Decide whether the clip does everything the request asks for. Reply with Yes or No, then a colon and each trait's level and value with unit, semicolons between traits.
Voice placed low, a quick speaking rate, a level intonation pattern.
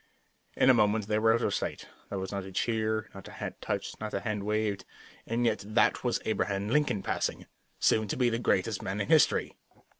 Yes: low, 110 Hz; fast, 215 wpm; narrow, 2.3 semitones